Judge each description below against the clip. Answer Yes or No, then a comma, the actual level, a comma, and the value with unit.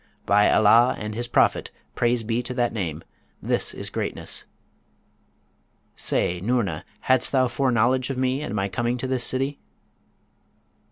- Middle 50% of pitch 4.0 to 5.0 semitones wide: No, average, 3.2 semitones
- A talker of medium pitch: No, low, 120 Hz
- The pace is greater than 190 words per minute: No, average, 145 wpm